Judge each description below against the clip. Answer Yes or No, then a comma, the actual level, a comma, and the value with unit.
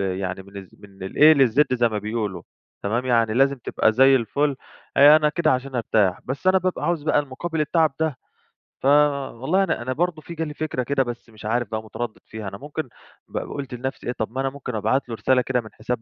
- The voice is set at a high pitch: No, low, 130 Hz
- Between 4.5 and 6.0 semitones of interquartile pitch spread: Yes, average, 4.9 semitones